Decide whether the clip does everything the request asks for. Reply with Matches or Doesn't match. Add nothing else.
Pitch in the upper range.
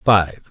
Doesn't match